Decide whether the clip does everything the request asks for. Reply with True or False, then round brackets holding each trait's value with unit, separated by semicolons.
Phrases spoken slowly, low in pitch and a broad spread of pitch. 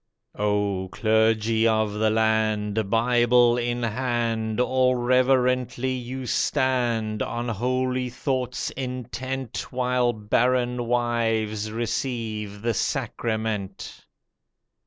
False (90 wpm; 120 Hz; 2.4 semitones)